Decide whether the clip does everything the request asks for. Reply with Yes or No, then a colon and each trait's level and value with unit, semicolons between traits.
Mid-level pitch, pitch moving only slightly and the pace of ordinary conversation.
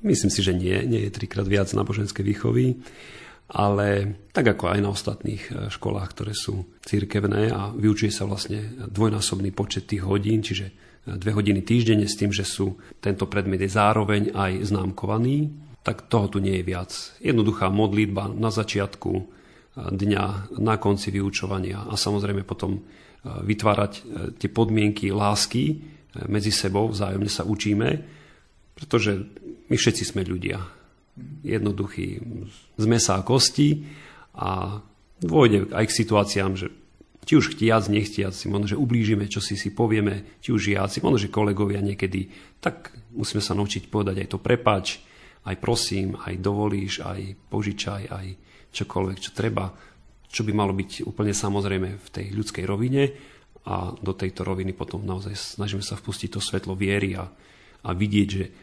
No: low, 100 Hz; narrow, 2.0 semitones; average, 150 wpm